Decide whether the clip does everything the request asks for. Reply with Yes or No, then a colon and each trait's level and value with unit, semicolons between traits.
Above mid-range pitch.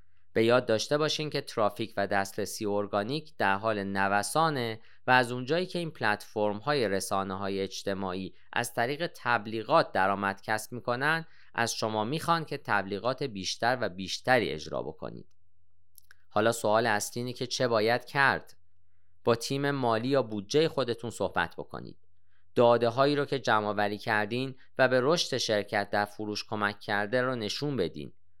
No: low, 110 Hz